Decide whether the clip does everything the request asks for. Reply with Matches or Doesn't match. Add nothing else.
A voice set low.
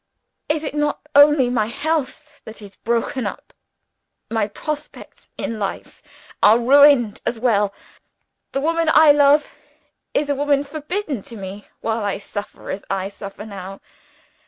Doesn't match